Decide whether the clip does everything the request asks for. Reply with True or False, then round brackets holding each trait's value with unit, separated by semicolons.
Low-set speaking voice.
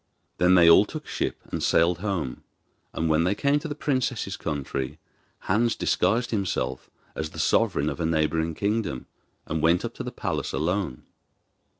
True (85 Hz)